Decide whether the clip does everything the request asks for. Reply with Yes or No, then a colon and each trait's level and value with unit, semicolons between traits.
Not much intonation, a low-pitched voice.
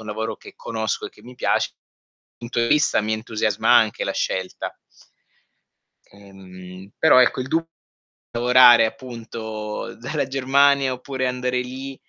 No: average, 3.0 semitones; low, 120 Hz